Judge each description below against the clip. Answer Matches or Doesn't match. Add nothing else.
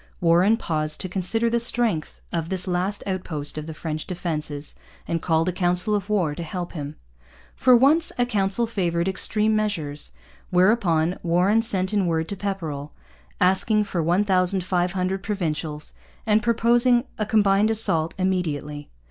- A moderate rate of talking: Matches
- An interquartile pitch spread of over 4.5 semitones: Doesn't match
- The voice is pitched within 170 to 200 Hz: Matches